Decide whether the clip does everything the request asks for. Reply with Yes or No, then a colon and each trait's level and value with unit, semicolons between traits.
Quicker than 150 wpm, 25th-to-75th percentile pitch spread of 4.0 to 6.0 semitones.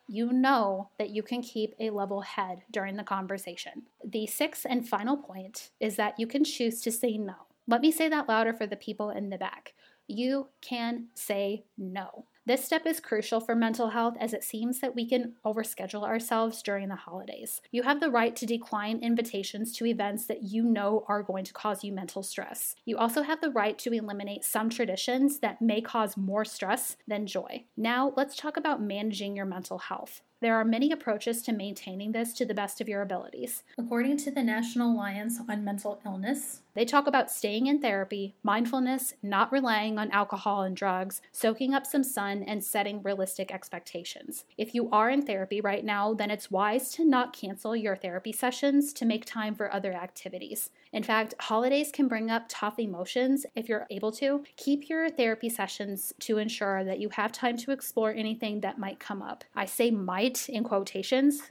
No: average, 195 wpm; average, 3.5 semitones